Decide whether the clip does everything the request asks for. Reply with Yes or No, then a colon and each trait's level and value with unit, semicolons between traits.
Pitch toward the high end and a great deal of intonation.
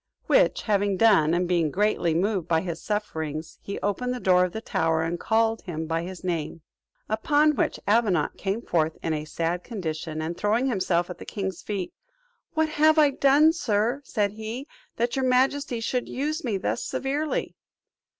Yes: high, 205 Hz; wide, 6.5 semitones